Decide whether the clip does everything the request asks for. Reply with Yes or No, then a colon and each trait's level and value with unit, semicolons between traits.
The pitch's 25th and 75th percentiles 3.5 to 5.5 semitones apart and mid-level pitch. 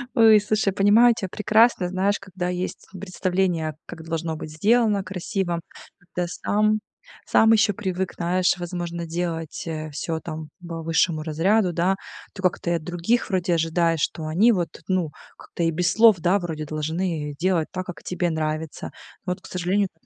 No: average, 2.9 semitones; medium, 180 Hz